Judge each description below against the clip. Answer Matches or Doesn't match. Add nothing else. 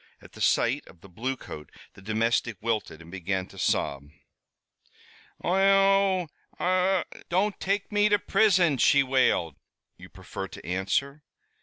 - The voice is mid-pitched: Doesn't match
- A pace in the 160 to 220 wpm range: Doesn't match